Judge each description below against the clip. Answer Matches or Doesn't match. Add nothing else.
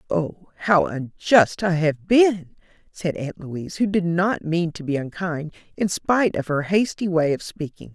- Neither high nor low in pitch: Matches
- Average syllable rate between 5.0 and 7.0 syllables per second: Doesn't match